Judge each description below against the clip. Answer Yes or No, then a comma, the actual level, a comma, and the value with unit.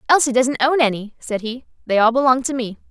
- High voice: Yes, very high, 250 Hz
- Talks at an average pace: No, fast, 225 wpm